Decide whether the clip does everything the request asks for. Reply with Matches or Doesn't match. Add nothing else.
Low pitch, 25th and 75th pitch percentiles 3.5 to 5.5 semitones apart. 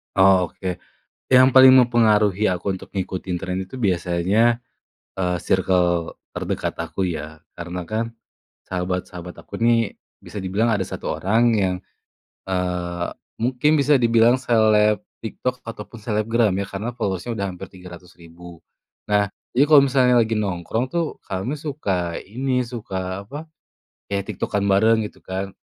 Matches